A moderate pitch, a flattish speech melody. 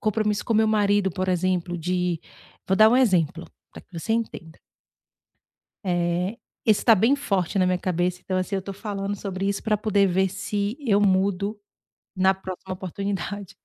No: high, 195 Hz; narrow, 2.2 semitones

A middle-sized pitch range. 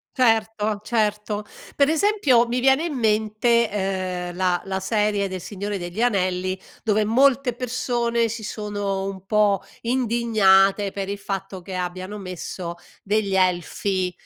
Yes: average, 3.5 semitones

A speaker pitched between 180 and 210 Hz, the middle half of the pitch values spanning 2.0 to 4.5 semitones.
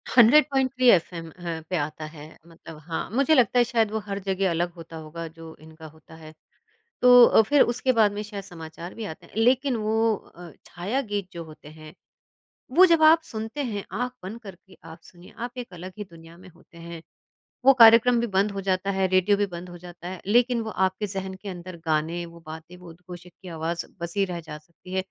No: medium, 185 Hz; average, 4.9 semitones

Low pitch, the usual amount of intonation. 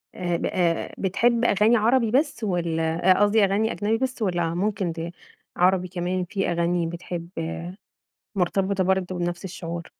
No: medium, 185 Hz; average, 3.3 semitones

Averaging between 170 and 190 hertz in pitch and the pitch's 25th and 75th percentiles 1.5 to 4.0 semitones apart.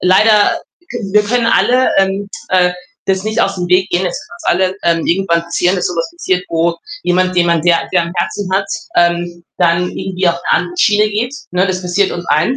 Yes: medium, 185 Hz; narrow, 2.4 semitones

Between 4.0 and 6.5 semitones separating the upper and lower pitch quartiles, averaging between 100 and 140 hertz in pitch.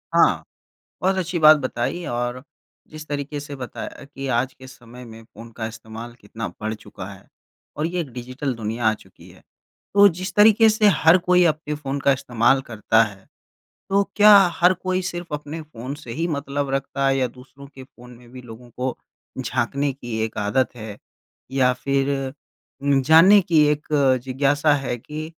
Yes: average, 4.3 semitones; low, 135 Hz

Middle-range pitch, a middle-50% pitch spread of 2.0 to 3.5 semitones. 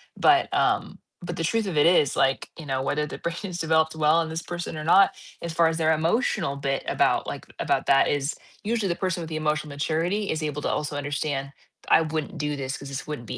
Yes: medium, 155 Hz; average, 2.9 semitones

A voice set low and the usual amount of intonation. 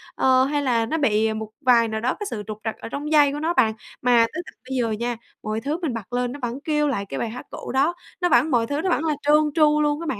No: very high, 255 Hz; average, 4.7 semitones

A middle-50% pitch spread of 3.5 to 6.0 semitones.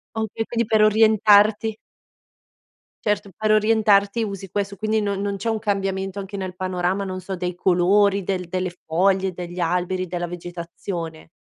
No: narrow, 2.5 semitones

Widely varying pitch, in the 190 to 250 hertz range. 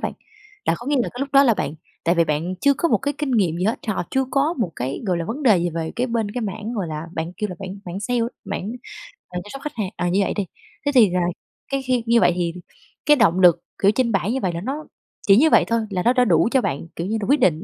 Yes: wide, 6.3 semitones; high, 210 Hz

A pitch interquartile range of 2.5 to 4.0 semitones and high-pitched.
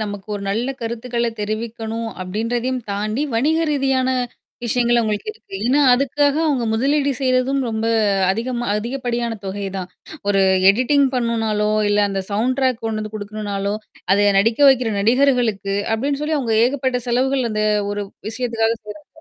Yes: average, 3.3 semitones; high, 235 Hz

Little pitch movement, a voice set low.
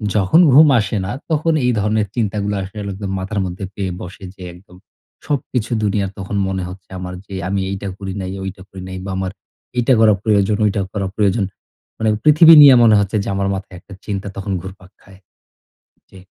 Yes: narrow, 2.2 semitones; low, 100 Hz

